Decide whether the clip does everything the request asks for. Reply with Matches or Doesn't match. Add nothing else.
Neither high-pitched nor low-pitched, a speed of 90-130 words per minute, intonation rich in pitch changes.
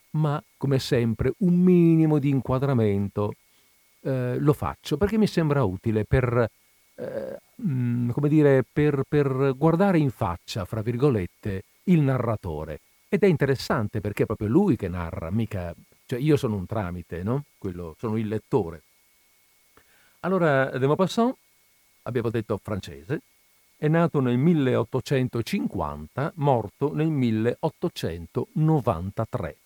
Doesn't match